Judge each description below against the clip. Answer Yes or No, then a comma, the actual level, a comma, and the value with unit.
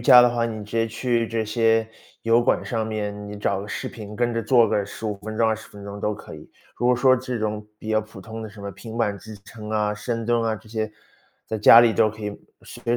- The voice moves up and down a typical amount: No, narrow, 1.7 semitones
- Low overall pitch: Yes, low, 110 Hz